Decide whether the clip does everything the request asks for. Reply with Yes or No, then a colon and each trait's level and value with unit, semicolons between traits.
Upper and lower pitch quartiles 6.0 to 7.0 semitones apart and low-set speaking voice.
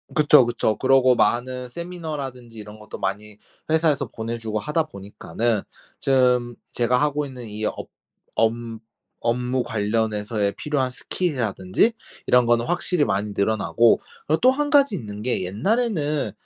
No: wide, 5.5 semitones; low, 125 Hz